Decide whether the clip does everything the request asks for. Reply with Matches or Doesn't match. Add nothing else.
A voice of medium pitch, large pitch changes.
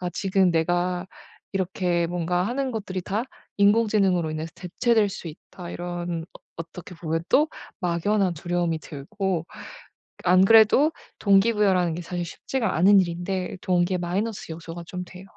Doesn't match